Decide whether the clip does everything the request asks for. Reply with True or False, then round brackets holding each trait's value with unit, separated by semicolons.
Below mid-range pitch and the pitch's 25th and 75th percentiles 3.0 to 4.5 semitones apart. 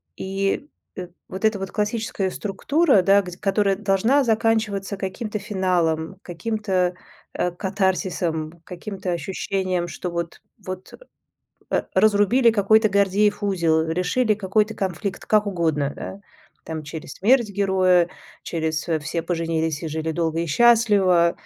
False (190 Hz; 3.4 semitones)